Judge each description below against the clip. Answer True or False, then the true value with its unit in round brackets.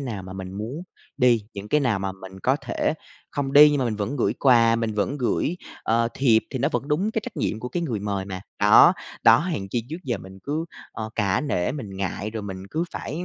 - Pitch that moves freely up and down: True (6.1 semitones)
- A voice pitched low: True (115 Hz)